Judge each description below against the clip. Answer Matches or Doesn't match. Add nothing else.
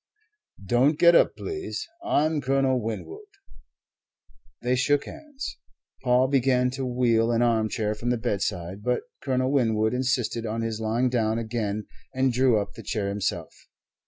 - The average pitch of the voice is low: Matches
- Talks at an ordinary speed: Matches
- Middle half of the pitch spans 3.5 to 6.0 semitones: Doesn't match